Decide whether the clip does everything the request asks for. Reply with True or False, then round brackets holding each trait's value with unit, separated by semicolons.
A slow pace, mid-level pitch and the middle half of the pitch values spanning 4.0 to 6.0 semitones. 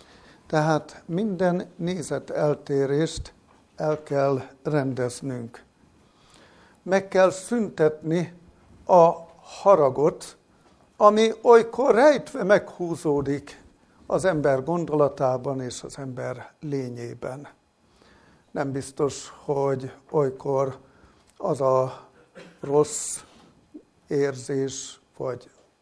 True (75 wpm; 145 Hz; 4.3 semitones)